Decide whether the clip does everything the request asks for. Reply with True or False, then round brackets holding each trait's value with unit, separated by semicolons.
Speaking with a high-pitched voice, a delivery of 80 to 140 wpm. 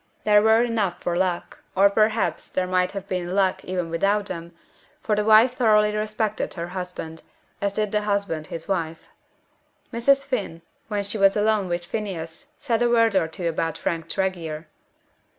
False (195 Hz; 170 wpm)